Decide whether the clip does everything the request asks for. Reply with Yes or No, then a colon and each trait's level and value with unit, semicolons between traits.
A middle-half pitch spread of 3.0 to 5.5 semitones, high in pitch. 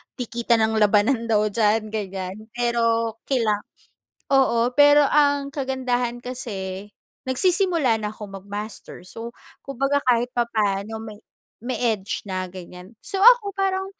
Yes: average, 4.1 semitones; high, 230 Hz